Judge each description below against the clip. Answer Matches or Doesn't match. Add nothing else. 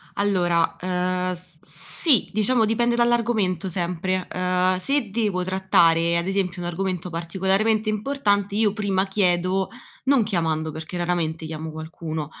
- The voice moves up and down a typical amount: Matches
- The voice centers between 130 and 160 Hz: Doesn't match